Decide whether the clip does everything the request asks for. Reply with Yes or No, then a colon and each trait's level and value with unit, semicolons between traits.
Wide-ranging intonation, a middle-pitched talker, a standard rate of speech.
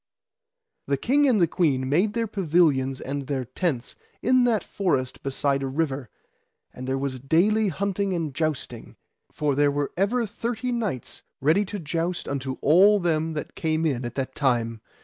Yes: wide, 6.7 semitones; medium, 155 Hz; average, 170 wpm